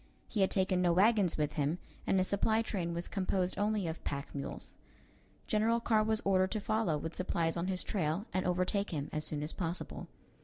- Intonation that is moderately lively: Yes, average, 3.8 semitones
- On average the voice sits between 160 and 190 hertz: Yes, medium, 185 Hz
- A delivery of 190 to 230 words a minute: Yes, average, 200 wpm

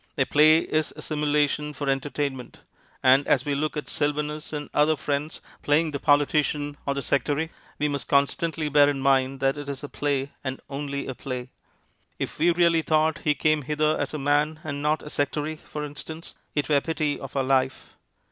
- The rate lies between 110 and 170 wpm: No, average, 195 wpm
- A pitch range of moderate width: No, narrow, 1.6 semitones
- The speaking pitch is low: No, medium, 145 Hz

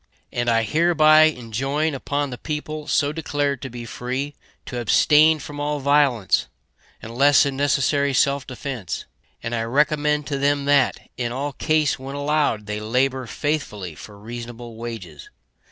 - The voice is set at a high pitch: No, medium, 140 Hz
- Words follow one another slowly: No, average, 150 wpm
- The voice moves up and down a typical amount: Yes, average, 3.6 semitones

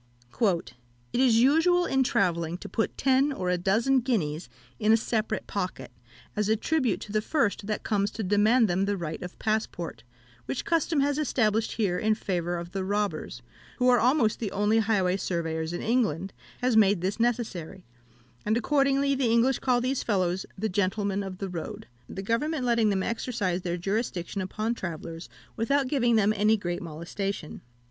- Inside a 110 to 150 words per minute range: No, average, 175 wpm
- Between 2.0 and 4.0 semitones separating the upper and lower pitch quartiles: No, average, 4.8 semitones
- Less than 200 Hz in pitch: No, high, 210 Hz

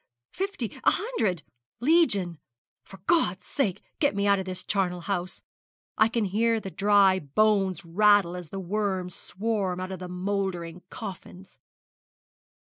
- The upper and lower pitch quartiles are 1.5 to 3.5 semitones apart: Yes, average, 2.8 semitones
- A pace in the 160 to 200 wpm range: No, average, 140 wpm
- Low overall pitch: No, high, 195 Hz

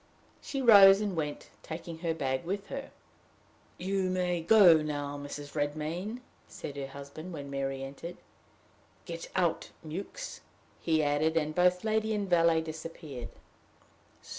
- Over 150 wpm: No, slow, 135 wpm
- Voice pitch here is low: No, medium, 165 Hz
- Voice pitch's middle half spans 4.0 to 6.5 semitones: Yes, average, 4.5 semitones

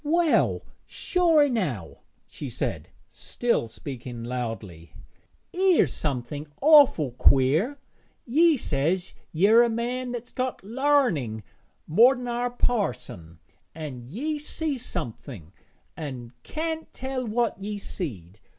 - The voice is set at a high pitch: Yes, high, 210 Hz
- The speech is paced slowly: Yes, slow, 105 wpm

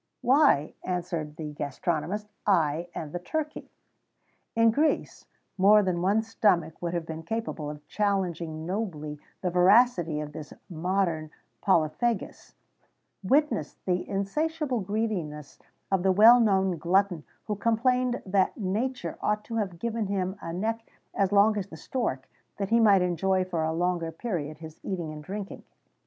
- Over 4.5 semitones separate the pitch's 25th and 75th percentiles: Yes, average, 4.9 semitones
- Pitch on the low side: No, high, 190 Hz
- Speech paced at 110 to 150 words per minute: Yes, average, 145 wpm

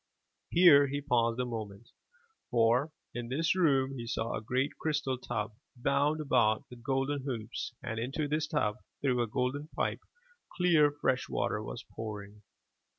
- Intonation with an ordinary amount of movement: Yes, average, 3.9 semitones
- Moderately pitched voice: No, low, 130 Hz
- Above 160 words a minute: No, average, 155 wpm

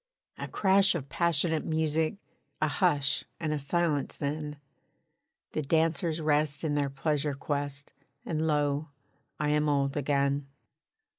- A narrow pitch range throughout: Yes, narrow, 2.0 semitones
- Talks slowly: Yes, slow, 130 wpm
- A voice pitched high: No, medium, 150 Hz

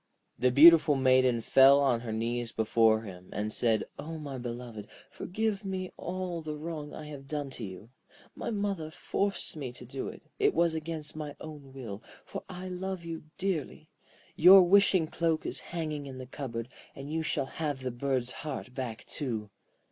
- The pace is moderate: Yes, average, 175 wpm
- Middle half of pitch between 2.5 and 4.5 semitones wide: No, average, 5.2 semitones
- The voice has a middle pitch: Yes, medium, 145 Hz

